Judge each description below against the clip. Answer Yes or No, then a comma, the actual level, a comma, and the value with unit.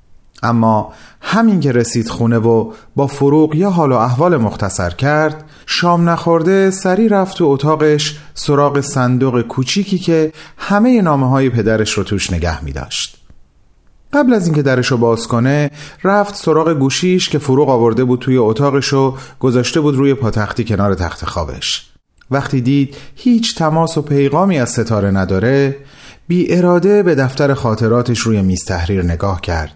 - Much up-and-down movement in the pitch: Yes, wide, 6.1 semitones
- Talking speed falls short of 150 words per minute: No, fast, 155 wpm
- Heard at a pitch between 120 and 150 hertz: Yes, low, 135 Hz